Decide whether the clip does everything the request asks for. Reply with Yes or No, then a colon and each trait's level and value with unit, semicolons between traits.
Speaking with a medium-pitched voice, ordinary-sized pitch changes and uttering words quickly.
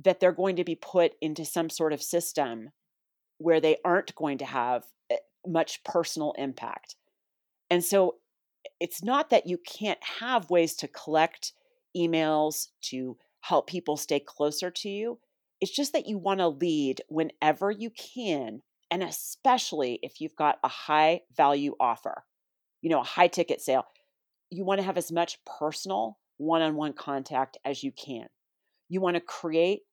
No: medium, 170 Hz; average, 4.2 semitones; average, 165 wpm